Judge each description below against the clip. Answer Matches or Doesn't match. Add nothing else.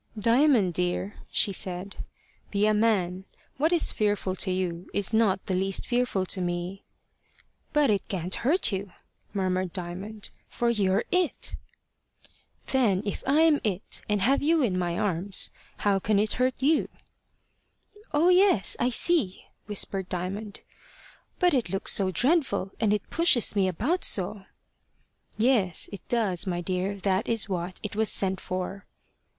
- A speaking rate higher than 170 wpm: Doesn't match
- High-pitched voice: Matches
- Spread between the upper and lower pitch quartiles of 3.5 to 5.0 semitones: Matches